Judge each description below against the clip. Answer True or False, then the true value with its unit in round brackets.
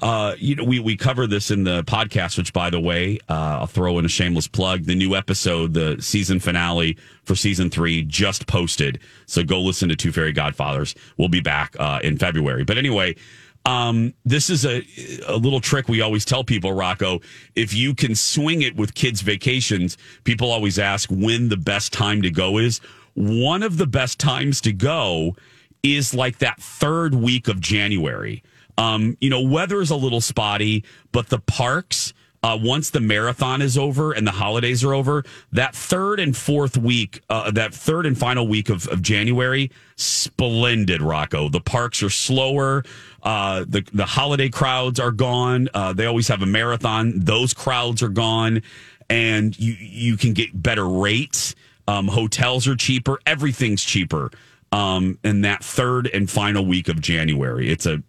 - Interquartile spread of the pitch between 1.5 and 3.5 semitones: False (4.5 semitones)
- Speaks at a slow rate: False (180 wpm)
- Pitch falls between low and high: False (115 Hz)